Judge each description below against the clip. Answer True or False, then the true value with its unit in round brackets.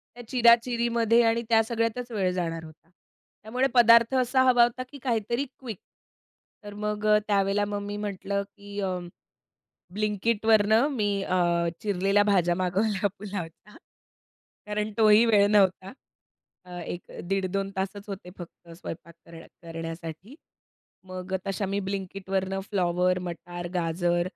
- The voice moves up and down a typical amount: True (3.5 semitones)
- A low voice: False (200 Hz)